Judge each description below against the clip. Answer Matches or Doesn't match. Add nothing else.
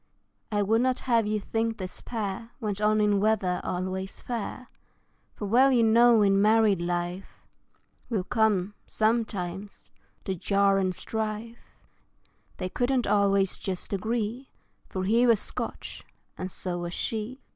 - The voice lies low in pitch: Doesn't match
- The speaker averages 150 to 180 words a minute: Doesn't match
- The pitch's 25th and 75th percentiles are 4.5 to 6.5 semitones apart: Doesn't match